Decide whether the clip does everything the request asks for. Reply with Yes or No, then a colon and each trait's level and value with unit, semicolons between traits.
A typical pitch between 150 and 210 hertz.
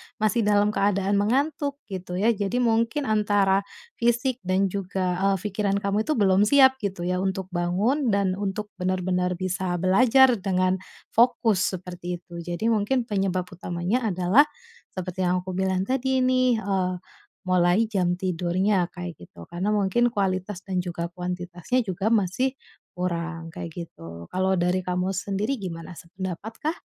Yes: high, 190 Hz